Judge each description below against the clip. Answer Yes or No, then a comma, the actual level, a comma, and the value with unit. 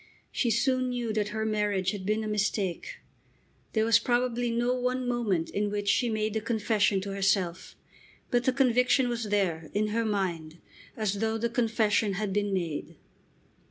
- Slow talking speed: No, average, 170 wpm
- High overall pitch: Yes, high, 215 Hz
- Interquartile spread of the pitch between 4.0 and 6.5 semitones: No, average, 3.0 semitones